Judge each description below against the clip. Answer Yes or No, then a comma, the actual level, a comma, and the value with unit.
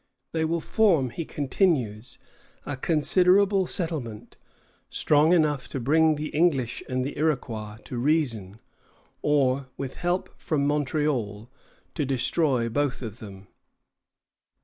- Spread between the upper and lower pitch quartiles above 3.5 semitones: Yes, average, 4.6 semitones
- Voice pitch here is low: No, medium, 145 Hz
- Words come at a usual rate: No, slow, 120 wpm